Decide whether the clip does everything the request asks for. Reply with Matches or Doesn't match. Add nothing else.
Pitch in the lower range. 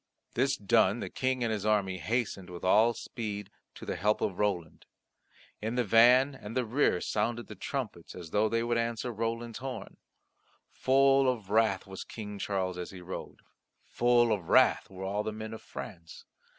Matches